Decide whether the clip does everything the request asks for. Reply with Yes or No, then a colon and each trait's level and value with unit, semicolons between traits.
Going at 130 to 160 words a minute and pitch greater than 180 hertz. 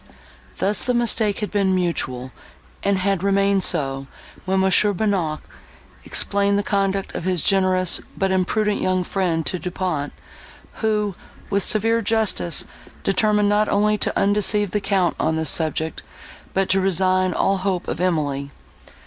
Yes: average, 150 wpm; high, 190 Hz